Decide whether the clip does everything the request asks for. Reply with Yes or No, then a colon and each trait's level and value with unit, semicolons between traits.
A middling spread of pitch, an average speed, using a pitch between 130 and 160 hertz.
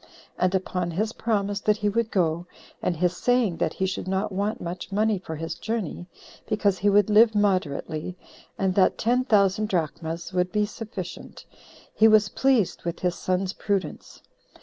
No: average, 3.0 semitones; average, 170 wpm; high, 195 Hz